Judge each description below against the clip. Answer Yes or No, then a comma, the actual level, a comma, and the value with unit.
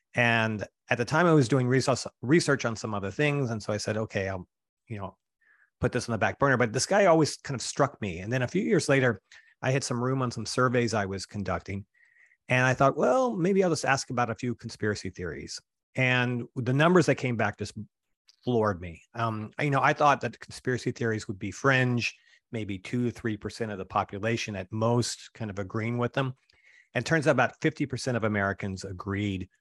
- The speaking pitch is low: Yes, low, 120 Hz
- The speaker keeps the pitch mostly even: No, average, 3.9 semitones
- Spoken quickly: Yes, fast, 220 wpm